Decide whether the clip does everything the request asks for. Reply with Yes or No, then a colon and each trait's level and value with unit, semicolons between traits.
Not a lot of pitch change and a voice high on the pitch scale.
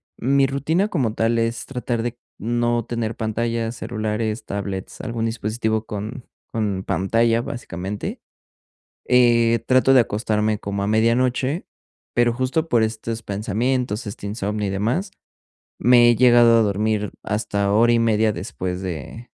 No: narrow, 2.3 semitones; low, 115 Hz